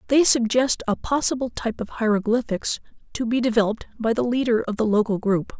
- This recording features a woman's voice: Yes, female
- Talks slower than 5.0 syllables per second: No, 5.9 syllables/s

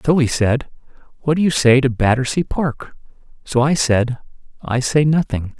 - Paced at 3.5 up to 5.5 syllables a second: Yes, 4.8 syllables/s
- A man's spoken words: Yes, male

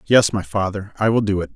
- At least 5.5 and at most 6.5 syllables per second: Yes, 5.7 syllables/s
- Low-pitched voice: Yes, low, 100 Hz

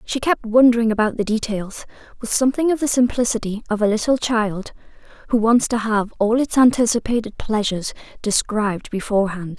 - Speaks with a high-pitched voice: Yes, high, 225 Hz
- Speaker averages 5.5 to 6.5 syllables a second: Yes, 5.6 syllables/s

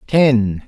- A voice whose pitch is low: Yes, low, 120 Hz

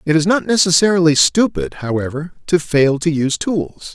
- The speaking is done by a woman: No, male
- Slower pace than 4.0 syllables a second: No, 5.1 syllables/s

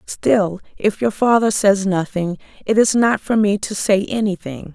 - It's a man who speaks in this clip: No, female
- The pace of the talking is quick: No, average, 175 wpm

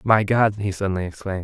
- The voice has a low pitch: Yes, low, 100 Hz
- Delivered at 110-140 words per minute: No, fast, 210 wpm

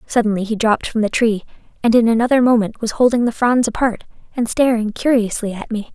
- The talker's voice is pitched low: No, high, 225 Hz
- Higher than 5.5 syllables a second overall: Yes, 6.0 syllables/s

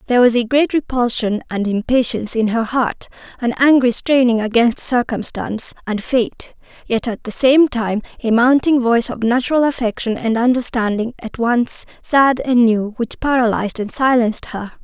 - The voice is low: No, high, 240 Hz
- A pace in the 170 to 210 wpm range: No, average, 160 wpm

